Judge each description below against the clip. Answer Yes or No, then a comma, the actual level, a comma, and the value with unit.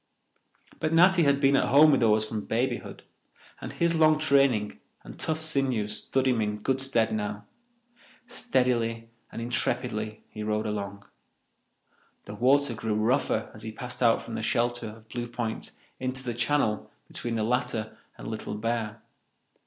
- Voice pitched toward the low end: Yes, low, 120 Hz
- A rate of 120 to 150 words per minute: No, average, 160 wpm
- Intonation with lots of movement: No, average, 3.8 semitones